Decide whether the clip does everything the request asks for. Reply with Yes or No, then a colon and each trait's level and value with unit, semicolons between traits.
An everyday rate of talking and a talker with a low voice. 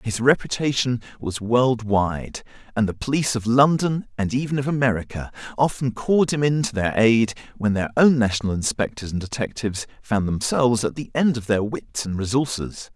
Yes: average, 170 wpm; low, 120 Hz